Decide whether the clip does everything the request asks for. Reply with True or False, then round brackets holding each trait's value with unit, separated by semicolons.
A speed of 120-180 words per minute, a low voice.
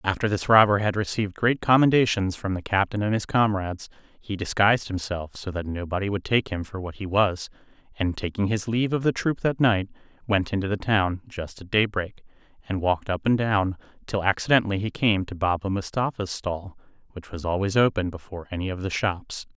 False (195 wpm; 100 Hz)